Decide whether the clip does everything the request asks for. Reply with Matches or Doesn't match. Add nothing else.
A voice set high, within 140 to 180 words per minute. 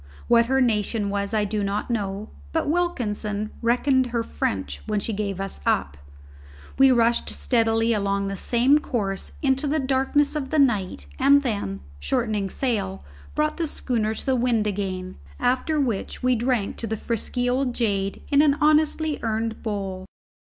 Matches